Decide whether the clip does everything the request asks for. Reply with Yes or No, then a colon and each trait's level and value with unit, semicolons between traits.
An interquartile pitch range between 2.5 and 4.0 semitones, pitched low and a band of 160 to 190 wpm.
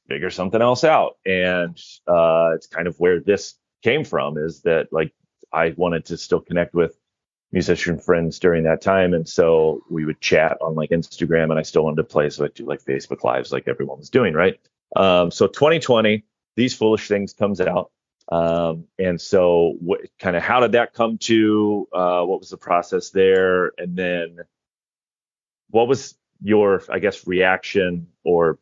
Yes: average, 3.3 semitones; very low, 90 Hz; average, 180 wpm